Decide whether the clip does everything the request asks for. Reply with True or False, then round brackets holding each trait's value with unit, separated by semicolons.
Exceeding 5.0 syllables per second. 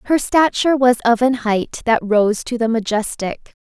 False (4.6 syllables/s)